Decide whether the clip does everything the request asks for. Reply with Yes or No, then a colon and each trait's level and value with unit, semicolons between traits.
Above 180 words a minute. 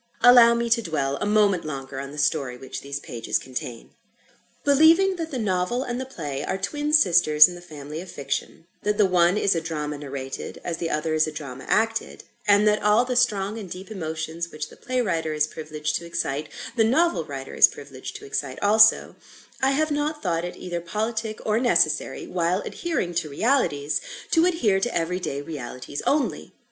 Yes: average, 195 wpm